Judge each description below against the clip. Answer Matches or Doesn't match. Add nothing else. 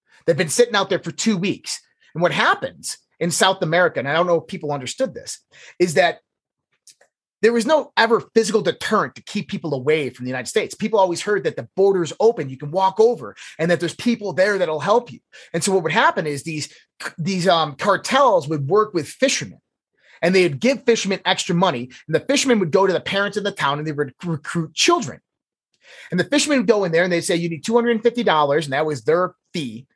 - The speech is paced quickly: Matches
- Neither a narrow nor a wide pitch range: Doesn't match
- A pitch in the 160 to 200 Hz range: Matches